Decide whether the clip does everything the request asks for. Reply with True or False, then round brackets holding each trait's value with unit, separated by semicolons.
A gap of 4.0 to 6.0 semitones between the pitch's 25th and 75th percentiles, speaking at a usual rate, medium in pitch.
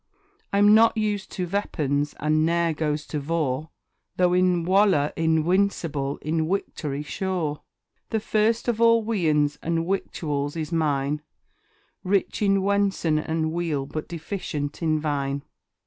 False (4.6 semitones; 130 wpm; 165 Hz)